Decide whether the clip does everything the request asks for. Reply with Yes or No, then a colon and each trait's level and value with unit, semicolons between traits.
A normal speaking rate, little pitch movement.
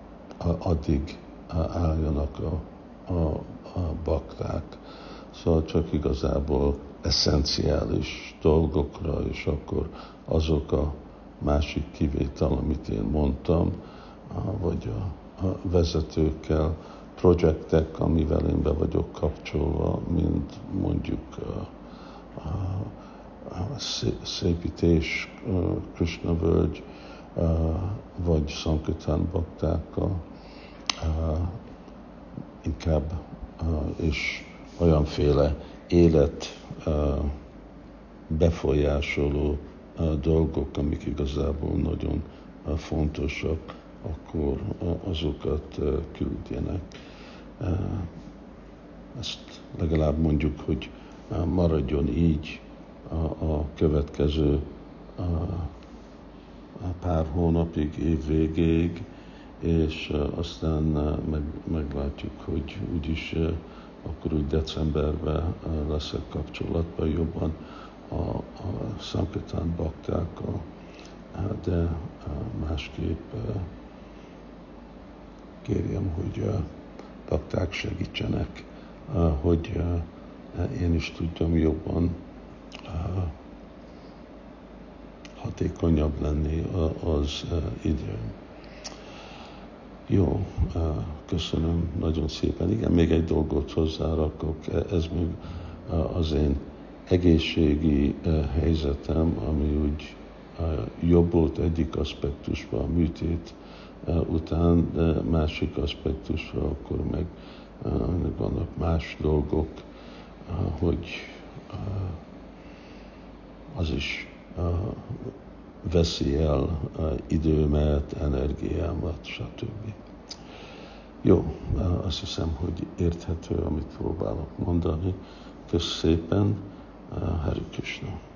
No: slow, 75 wpm; narrow, 2.2 semitones